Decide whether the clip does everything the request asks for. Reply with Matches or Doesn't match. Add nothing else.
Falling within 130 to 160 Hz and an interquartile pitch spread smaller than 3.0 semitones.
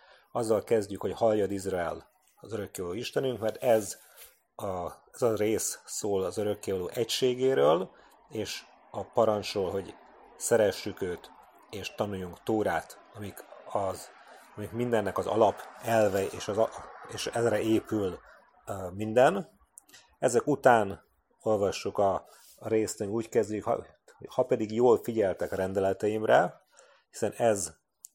Doesn't match